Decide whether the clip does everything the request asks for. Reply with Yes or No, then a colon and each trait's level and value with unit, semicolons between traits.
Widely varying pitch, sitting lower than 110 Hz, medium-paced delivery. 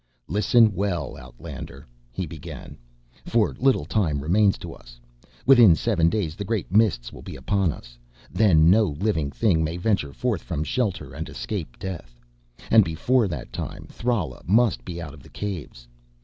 Yes: wide, 5.8 semitones; very low, 90 Hz; average, 165 wpm